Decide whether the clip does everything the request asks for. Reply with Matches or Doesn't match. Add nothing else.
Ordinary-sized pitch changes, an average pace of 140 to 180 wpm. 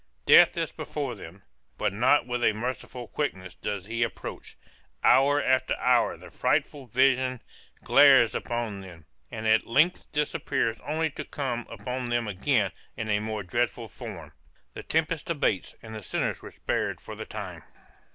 Matches